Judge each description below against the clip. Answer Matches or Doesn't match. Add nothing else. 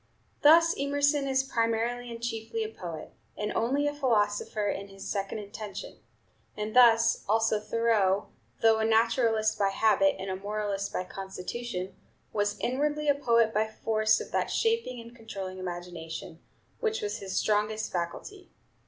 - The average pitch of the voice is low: Doesn't match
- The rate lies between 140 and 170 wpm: Matches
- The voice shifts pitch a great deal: Doesn't match